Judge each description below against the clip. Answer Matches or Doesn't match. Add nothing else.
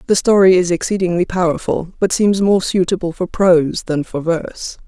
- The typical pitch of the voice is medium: Matches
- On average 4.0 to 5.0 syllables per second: Doesn't match